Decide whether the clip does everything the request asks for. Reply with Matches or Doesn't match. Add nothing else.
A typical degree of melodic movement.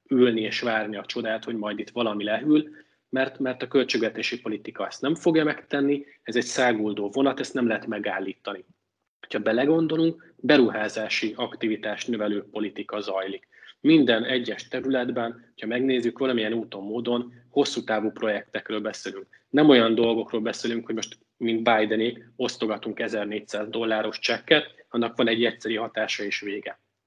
Matches